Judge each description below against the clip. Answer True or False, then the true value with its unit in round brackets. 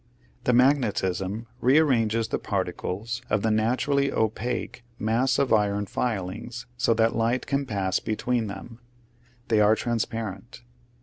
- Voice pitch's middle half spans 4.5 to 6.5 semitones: False (2.7 semitones)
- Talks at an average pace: False (130 wpm)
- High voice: False (115 Hz)